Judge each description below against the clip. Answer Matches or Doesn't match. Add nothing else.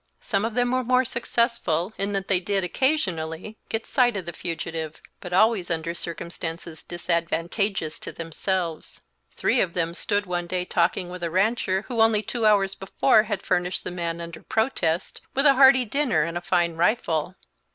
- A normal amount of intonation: Matches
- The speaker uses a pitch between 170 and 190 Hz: Matches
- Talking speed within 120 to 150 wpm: Doesn't match